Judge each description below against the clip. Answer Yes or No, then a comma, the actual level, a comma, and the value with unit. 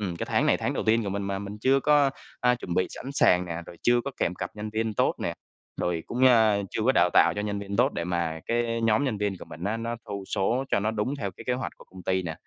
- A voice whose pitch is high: No, low, 105 Hz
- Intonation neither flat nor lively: Yes, average, 4.1 semitones